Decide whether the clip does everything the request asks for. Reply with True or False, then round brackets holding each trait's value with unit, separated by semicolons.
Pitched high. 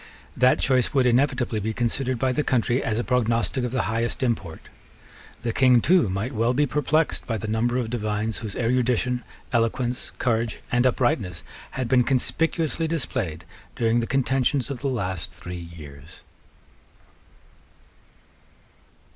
False (120 Hz)